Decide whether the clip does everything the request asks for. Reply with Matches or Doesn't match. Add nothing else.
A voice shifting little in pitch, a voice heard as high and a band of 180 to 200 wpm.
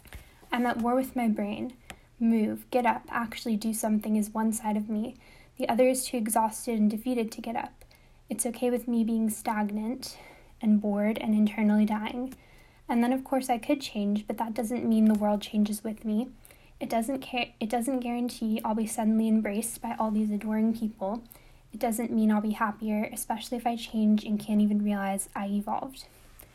Matches